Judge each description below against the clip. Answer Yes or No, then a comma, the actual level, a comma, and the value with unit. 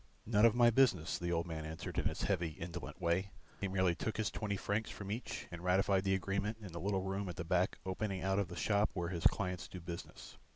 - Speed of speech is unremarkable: No, fast, 240 wpm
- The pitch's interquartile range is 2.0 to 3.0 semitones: Yes, average, 2.7 semitones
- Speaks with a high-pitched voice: No, very low, 95 Hz